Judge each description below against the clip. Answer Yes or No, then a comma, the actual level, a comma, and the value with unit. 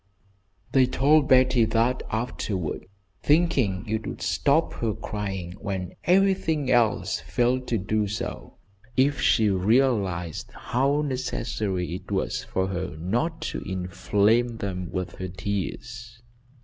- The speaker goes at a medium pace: No, slow, 125 wpm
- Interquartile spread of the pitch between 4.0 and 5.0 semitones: No, wide, 5.4 semitones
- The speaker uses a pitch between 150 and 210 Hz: No, low, 110 Hz